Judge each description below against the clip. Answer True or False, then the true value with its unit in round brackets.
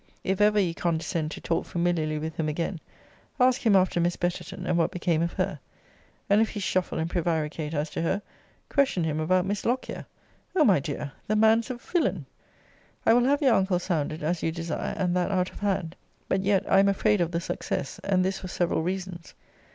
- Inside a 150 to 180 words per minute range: False (205 wpm)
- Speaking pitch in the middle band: True (180 Hz)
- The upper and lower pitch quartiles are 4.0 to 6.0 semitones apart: False (3.3 semitones)